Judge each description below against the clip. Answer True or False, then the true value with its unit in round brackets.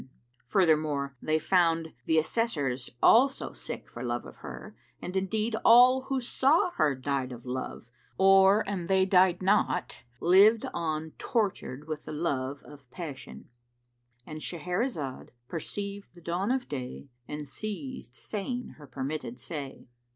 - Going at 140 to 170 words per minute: True (145 wpm)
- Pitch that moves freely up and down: True (6.0 semitones)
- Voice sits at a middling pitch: True (170 Hz)